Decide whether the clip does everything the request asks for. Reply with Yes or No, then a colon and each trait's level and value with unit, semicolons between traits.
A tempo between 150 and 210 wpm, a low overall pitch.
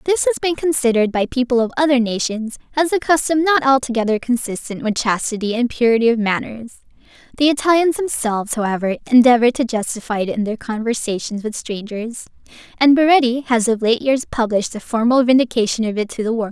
No: average, 180 wpm; high, 245 Hz